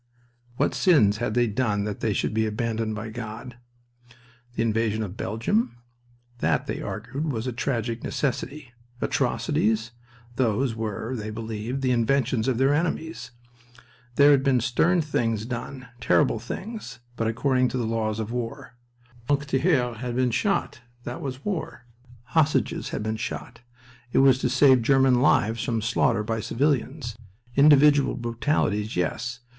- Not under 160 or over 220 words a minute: No, average, 150 wpm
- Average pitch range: Yes, average, 3.4 semitones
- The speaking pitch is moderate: No, low, 120 Hz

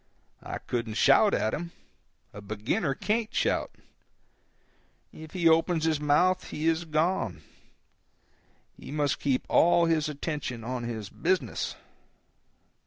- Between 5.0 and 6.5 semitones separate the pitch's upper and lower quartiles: Yes, wide, 5.4 semitones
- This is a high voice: No, medium, 150 Hz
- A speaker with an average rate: No, slow, 115 wpm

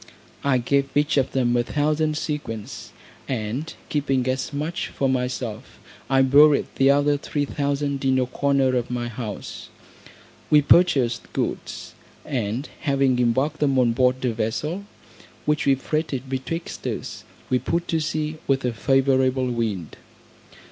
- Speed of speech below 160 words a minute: Yes, average, 145 wpm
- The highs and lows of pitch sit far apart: No, average, 2.8 semitones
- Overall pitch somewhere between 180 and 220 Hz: No, low, 135 Hz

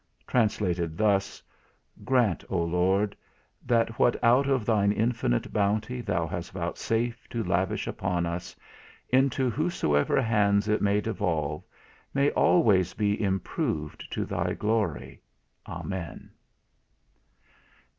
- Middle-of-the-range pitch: No, low, 105 Hz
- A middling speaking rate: No, slow, 110 wpm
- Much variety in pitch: No, average, 4.6 semitones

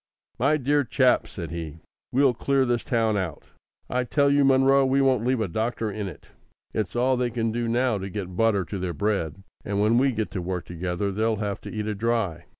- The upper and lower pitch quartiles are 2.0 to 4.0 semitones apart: No, average, 4.5 semitones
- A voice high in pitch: No, low, 110 Hz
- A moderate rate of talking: No, fast, 220 wpm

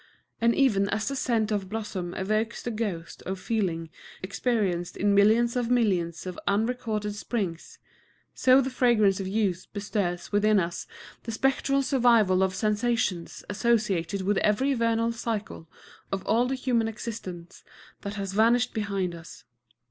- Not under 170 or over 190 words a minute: No, average, 150 wpm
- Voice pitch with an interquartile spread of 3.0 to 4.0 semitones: Yes, average, 3.5 semitones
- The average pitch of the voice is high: Yes, high, 210 Hz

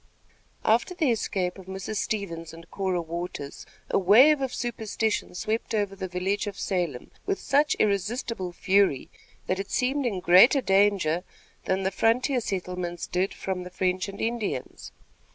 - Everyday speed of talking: Yes, average, 150 wpm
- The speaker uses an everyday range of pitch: Yes, average, 3.7 semitones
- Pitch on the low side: No, high, 195 Hz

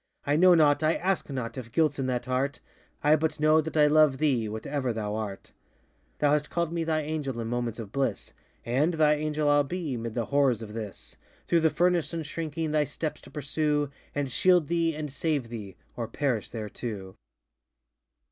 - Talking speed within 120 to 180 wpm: No, average, 190 wpm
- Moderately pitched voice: Yes, medium, 145 Hz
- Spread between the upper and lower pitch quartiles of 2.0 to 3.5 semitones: No, average, 4.5 semitones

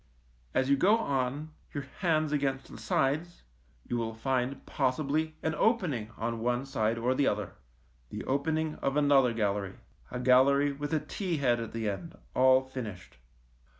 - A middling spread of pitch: Yes, average, 4.1 semitones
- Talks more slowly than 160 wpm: No, average, 165 wpm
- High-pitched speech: No, low, 135 Hz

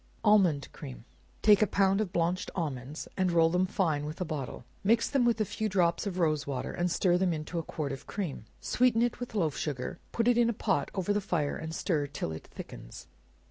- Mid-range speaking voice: Yes, medium, 175 Hz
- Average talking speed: No, fast, 225 wpm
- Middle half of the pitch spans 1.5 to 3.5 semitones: No, average, 5.1 semitones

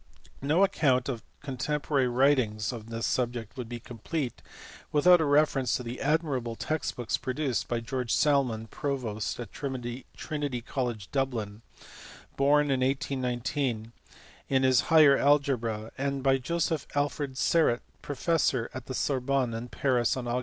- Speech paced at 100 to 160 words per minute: Yes, average, 145 wpm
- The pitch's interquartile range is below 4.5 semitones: Yes, average, 3.0 semitones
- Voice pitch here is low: Yes, low, 130 Hz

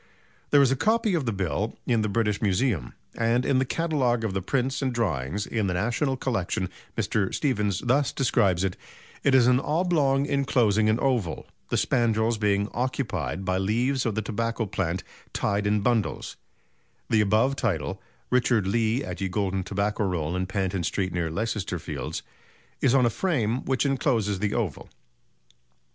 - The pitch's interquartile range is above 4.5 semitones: Yes, average, 4.9 semitones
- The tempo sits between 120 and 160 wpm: No, average, 170 wpm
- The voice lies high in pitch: No, low, 110 Hz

